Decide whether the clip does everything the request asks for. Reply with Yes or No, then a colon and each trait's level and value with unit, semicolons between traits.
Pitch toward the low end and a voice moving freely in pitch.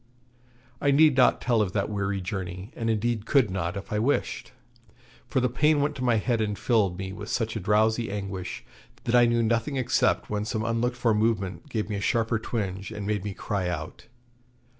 No: low, 110 Hz; average, 3.2 semitones